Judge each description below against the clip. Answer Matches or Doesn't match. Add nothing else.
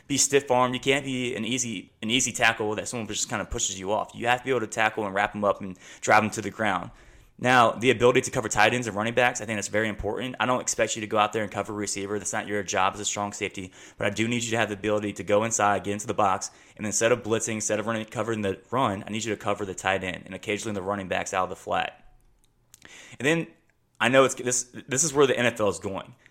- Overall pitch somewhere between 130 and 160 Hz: Doesn't match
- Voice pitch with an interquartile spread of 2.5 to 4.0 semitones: Matches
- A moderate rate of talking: Doesn't match